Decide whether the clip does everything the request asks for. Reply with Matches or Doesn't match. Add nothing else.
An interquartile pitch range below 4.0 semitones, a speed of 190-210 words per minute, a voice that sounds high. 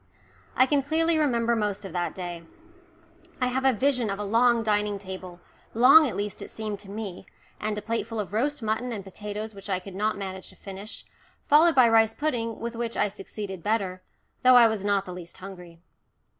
Matches